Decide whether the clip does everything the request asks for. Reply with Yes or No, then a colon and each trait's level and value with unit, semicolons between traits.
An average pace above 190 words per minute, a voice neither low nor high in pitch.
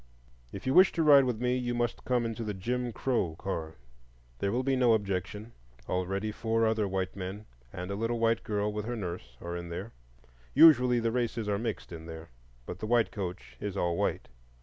No: average, 200 wpm; low, 110 Hz